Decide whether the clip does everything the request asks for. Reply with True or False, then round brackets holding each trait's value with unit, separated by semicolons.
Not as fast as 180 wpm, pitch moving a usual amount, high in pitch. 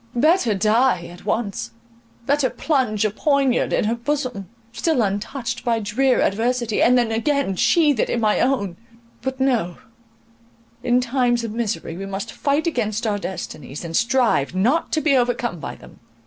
True (160 wpm; 4.3 semitones; 235 Hz)